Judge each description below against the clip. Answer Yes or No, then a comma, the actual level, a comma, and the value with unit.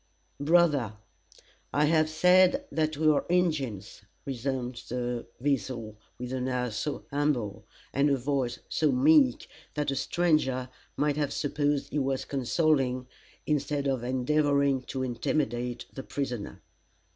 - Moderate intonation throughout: Yes, average, 3.2 semitones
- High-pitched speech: No, medium, 140 Hz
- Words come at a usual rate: No, slow, 130 wpm